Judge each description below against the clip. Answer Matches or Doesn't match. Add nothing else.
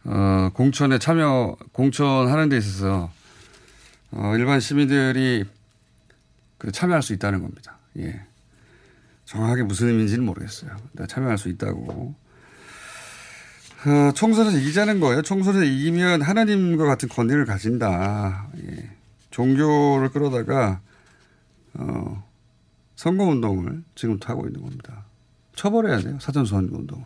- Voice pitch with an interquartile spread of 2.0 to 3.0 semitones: Doesn't match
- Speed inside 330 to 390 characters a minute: Doesn't match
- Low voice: Matches